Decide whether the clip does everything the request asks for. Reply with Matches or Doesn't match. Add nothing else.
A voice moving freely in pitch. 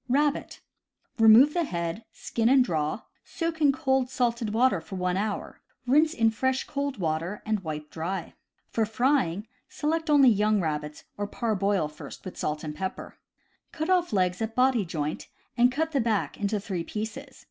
Matches